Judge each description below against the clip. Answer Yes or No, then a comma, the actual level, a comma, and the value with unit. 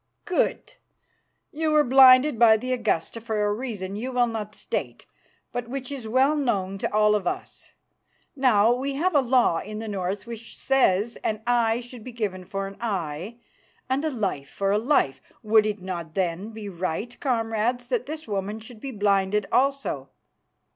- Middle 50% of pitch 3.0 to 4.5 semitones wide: Yes, average, 4.2 semitones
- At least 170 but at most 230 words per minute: Yes, average, 180 wpm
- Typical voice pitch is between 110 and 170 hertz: No, high, 225 Hz